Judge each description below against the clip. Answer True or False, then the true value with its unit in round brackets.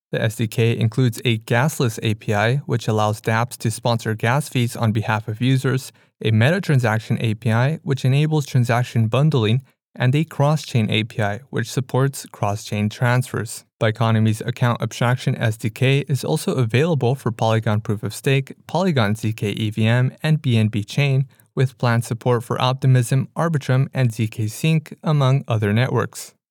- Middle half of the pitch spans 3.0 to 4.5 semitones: True (3.3 semitones)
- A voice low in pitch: True (120 Hz)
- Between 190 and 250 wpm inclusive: False (145 wpm)